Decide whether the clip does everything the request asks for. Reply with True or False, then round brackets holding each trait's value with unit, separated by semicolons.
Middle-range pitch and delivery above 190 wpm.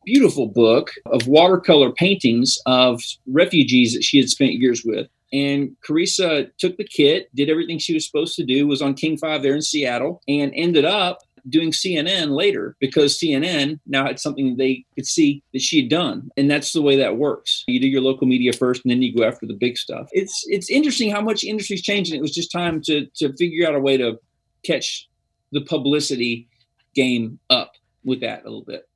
True (145 Hz; 205 wpm)